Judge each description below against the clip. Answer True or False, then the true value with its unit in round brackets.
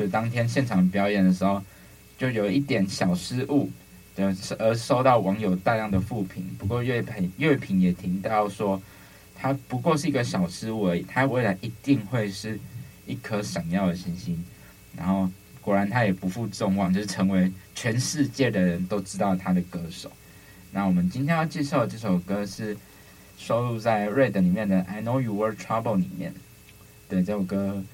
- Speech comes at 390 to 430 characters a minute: False (290 characters per minute)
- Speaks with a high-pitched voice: False (100 Hz)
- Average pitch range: True (4.8 semitones)